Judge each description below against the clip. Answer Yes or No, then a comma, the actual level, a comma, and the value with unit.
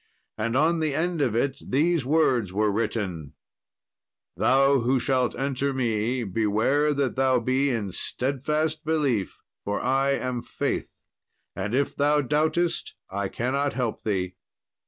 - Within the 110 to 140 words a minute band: Yes, slow, 135 wpm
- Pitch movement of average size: Yes, average, 4.1 semitones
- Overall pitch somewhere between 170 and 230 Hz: No, low, 130 Hz